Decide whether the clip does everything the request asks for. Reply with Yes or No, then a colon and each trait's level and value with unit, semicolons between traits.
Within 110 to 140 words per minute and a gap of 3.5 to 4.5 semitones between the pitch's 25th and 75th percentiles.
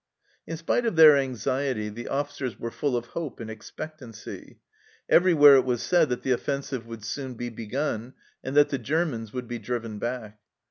No: average, 180 wpm; average, 3.8 semitones